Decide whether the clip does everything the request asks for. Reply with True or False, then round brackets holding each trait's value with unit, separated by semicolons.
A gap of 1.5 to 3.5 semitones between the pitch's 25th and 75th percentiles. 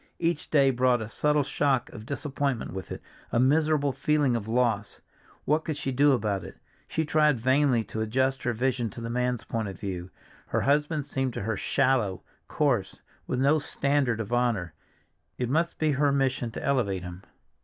False (4.2 semitones)